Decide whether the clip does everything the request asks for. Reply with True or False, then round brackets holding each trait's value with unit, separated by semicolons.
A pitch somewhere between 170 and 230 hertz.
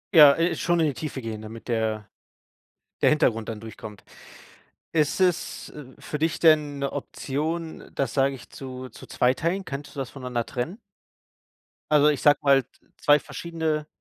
False (140 Hz)